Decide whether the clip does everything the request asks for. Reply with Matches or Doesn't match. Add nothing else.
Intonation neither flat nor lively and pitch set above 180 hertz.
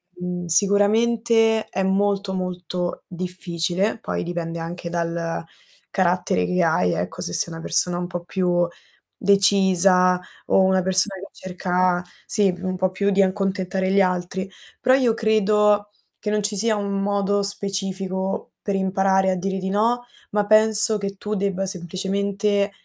Doesn't match